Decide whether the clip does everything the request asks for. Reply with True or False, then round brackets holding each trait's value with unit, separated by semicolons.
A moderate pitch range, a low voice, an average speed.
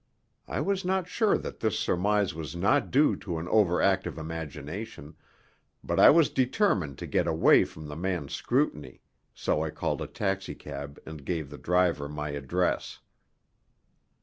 False (5.9 semitones; 90 Hz; 155 wpm)